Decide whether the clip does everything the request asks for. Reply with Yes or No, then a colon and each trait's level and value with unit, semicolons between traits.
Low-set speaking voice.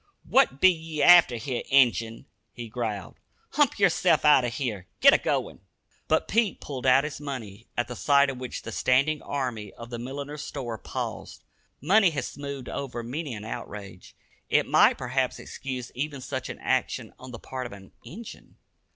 Yes: low, 130 Hz